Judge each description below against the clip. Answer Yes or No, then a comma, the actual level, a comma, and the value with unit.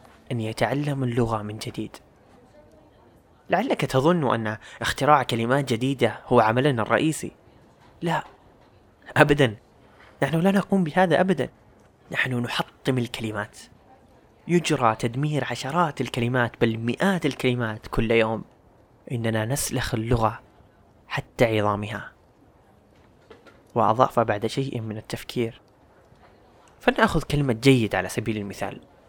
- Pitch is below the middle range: Yes, low, 120 Hz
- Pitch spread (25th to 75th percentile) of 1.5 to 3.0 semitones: No, average, 4.0 semitones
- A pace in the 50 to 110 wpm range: Yes, average, 100 wpm